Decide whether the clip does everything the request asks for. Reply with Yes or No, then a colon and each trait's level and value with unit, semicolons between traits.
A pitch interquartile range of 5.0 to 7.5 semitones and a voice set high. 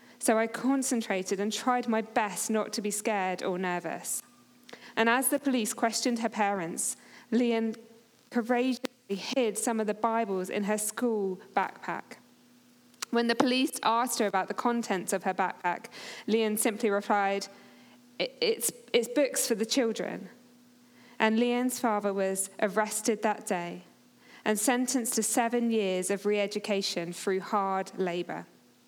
No: average, 3.3 semitones; high, 225 Hz